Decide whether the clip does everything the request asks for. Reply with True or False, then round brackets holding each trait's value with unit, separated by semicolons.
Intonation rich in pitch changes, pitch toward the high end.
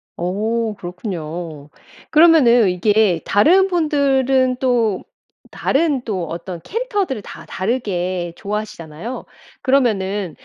True (6.6 semitones; 215 Hz)